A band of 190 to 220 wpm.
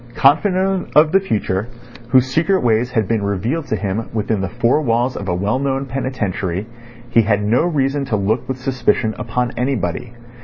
No: average, 180 wpm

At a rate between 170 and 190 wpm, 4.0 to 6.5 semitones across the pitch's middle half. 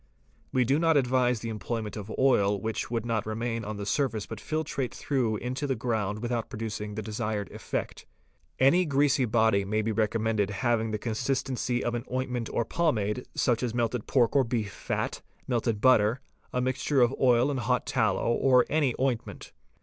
No: average, 180 wpm; average, 3.0 semitones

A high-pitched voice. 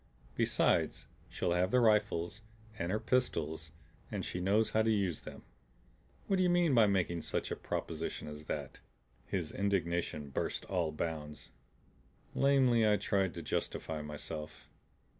No: very low, 90 Hz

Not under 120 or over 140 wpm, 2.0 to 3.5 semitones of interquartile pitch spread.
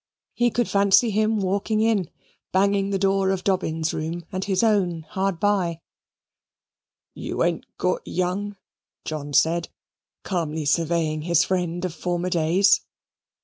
Yes: slow, 135 wpm; average, 3.1 semitones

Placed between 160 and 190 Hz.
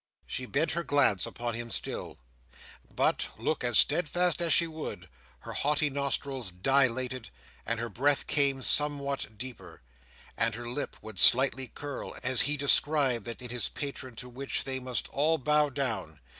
No: low, 130 Hz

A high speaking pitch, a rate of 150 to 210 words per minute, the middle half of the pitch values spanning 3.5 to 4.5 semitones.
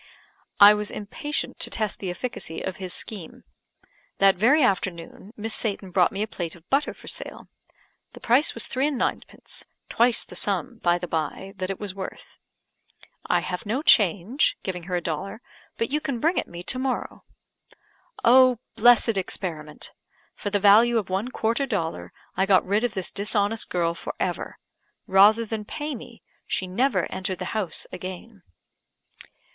Yes: high, 205 Hz; average, 170 wpm; average, 4.2 semitones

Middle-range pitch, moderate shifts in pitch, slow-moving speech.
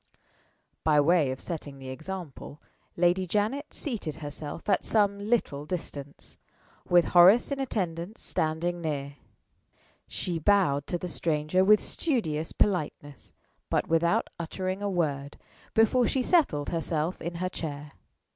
Yes: medium, 170 Hz; average, 4.9 semitones; slow, 130 wpm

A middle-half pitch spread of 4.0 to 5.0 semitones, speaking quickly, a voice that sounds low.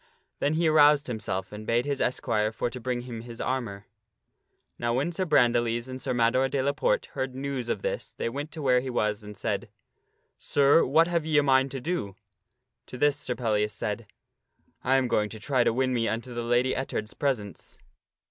No: average, 3.3 semitones; fast, 215 wpm; low, 125 Hz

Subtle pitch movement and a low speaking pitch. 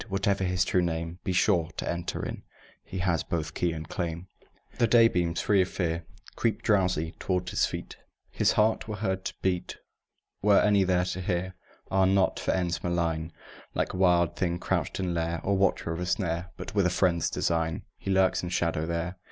Yes: narrow, 2.1 semitones; very low, 90 Hz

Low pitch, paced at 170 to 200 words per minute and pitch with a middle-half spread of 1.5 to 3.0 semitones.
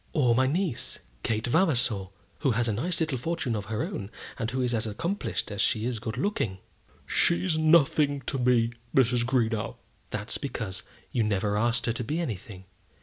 No: low, 120 Hz; average, 180 wpm; average, 4.5 semitones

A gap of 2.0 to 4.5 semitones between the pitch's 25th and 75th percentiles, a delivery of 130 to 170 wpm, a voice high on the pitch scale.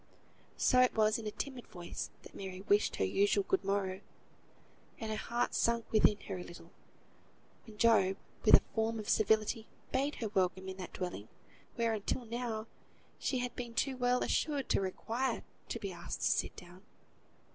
No: average, 3.6 semitones; average, 180 wpm; high, 215 Hz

